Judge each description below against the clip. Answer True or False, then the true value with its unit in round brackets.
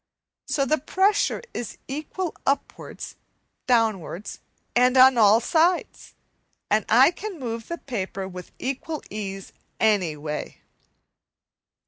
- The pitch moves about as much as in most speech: False (6.7 semitones)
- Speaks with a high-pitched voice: True (240 Hz)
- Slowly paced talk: True (110 wpm)